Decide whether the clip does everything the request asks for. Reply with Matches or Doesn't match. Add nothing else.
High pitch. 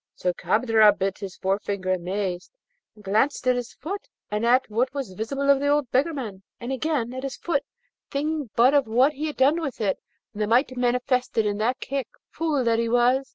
Matches